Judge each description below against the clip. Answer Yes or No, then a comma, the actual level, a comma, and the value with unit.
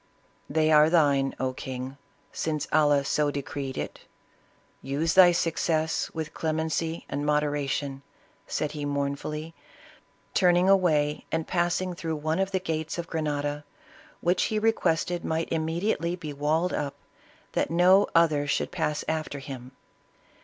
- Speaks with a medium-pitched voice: Yes, medium, 155 Hz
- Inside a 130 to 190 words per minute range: Yes, slow, 135 wpm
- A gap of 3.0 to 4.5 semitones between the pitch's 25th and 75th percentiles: No, narrow, 2.6 semitones